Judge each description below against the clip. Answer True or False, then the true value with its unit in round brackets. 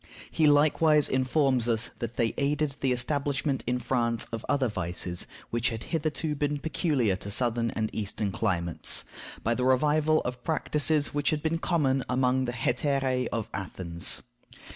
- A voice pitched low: True (130 Hz)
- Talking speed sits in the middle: True (155 wpm)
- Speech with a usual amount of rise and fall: True (4.2 semitones)